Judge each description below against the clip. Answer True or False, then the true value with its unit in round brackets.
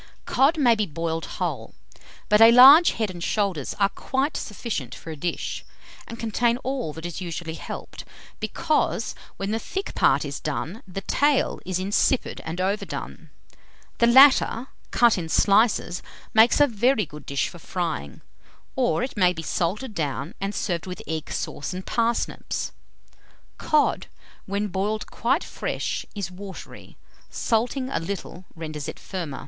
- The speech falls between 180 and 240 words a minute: False (155 wpm)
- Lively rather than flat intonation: True (5.7 semitones)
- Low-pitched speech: False (200 Hz)